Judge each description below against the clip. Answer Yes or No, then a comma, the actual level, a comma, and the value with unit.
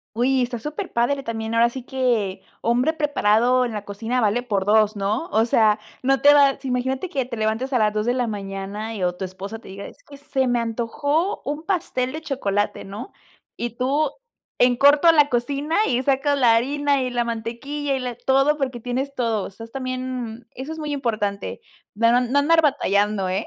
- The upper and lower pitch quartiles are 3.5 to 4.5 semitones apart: Yes, average, 3.9 semitones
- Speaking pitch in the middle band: No, high, 245 Hz